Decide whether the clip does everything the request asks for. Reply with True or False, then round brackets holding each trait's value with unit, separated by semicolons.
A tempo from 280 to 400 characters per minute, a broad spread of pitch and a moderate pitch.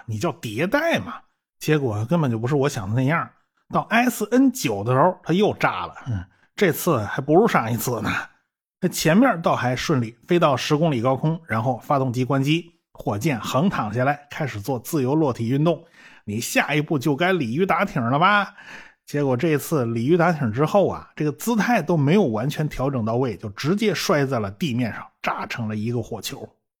True (285 characters per minute; 6.0 semitones; 145 Hz)